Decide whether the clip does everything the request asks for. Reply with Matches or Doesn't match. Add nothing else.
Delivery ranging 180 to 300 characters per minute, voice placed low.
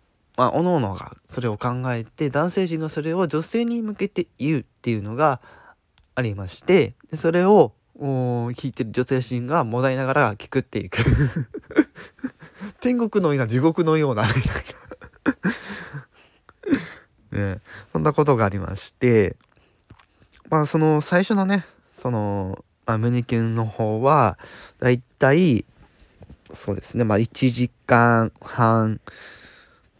Matches